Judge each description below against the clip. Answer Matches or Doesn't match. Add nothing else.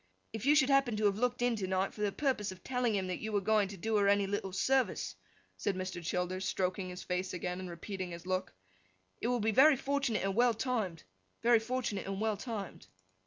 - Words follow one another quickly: Matches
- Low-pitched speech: Doesn't match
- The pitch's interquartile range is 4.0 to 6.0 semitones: Matches